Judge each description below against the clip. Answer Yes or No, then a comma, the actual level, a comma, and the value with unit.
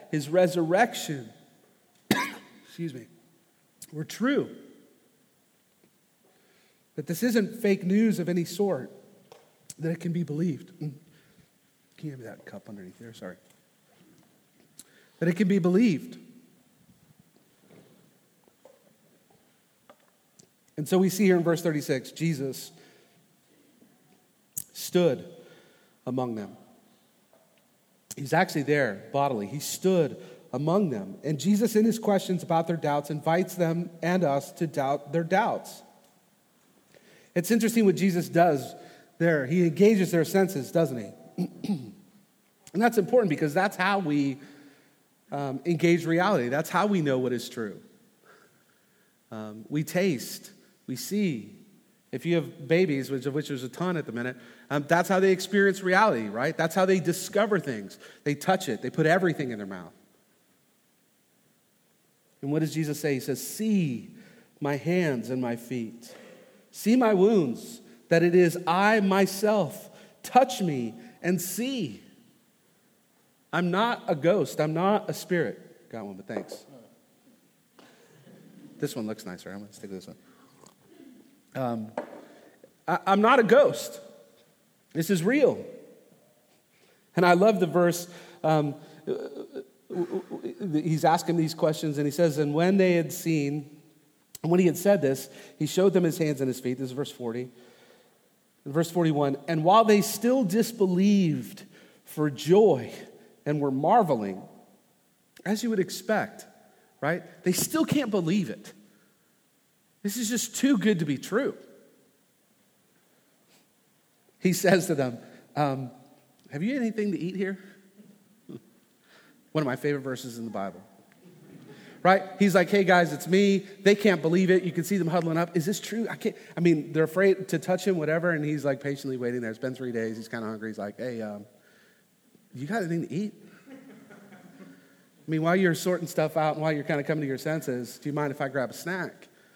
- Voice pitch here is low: No, medium, 170 Hz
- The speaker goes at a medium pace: Yes, average, 155 wpm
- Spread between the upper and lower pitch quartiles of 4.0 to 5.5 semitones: Yes, average, 5.2 semitones